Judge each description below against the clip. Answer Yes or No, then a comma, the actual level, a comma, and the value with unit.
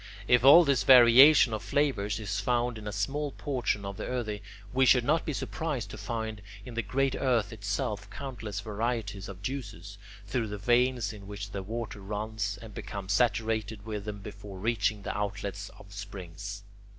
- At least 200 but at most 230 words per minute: No, average, 175 wpm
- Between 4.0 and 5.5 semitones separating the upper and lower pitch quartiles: No, average, 3.3 semitones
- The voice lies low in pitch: Yes, low, 110 Hz